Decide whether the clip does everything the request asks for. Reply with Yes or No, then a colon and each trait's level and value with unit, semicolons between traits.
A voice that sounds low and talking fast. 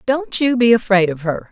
No: high, 215 Hz; fast, 240 wpm